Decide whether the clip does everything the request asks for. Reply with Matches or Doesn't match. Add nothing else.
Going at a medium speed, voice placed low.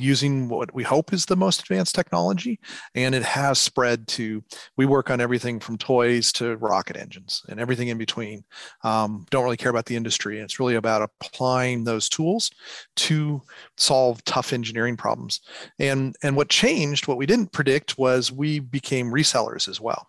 Matches